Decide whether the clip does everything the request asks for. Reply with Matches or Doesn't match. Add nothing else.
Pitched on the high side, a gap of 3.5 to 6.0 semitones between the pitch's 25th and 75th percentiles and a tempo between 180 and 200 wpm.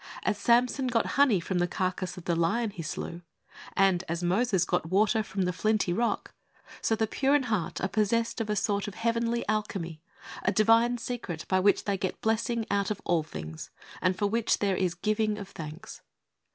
Matches